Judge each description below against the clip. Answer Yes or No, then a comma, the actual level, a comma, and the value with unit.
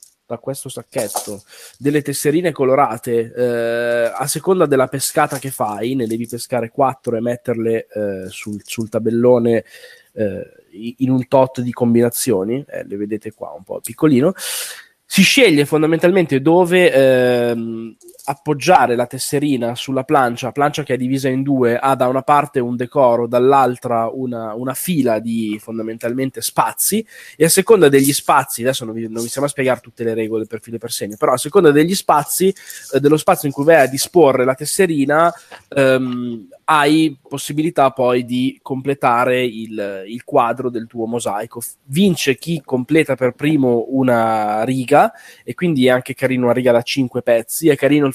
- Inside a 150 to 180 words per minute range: Yes, average, 165 wpm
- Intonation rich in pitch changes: No, average, 3.5 semitones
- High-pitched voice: No, low, 130 Hz